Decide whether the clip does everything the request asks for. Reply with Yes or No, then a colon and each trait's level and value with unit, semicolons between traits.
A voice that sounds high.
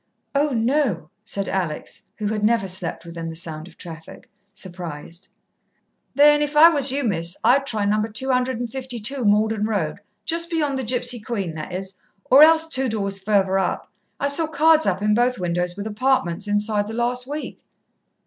Yes: high, 215 Hz